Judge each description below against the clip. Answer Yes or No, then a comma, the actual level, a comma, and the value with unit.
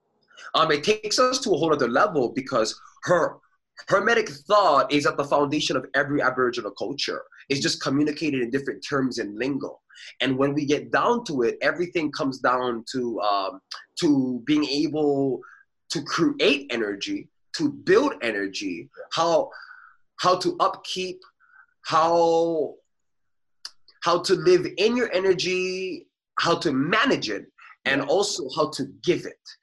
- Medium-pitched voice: Yes, medium, 180 Hz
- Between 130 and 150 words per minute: Yes, average, 145 wpm